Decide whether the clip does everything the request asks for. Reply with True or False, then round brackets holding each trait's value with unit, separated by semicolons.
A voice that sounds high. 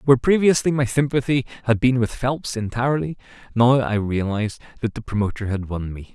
False (120 Hz)